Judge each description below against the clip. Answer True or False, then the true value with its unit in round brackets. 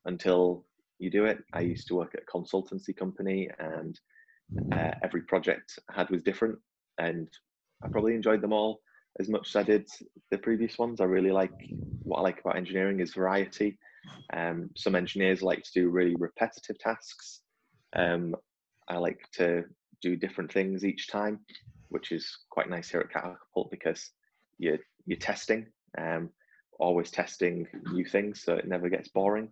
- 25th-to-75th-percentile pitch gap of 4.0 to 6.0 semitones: False (2.8 semitones)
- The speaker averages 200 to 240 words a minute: False (170 wpm)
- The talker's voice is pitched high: False (95 Hz)